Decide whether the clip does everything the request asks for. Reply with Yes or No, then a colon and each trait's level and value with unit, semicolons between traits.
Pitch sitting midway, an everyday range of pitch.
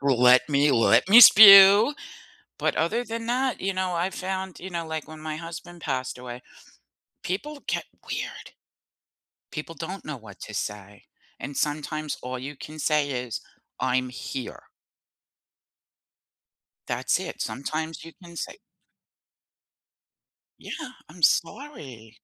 No: medium, 155 Hz; wide, 6.4 semitones